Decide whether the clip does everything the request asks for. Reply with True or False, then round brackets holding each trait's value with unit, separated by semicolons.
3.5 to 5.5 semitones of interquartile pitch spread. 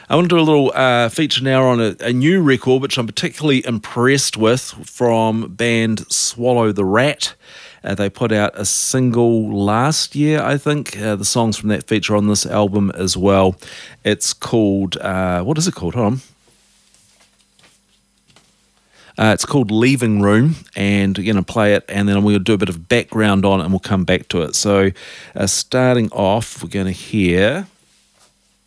True (4.3 semitones)